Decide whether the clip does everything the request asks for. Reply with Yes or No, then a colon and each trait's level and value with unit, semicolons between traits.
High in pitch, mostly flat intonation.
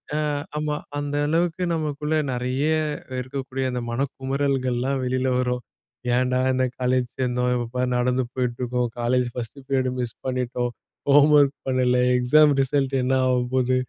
No: low, 130 Hz; narrow, 1.8 semitones